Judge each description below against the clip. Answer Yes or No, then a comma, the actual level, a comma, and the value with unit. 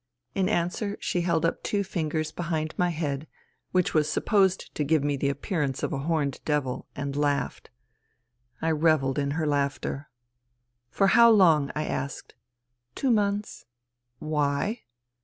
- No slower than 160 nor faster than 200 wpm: Yes, average, 165 wpm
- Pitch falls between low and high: Yes, medium, 155 Hz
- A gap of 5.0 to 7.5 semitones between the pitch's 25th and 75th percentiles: No, average, 3.9 semitones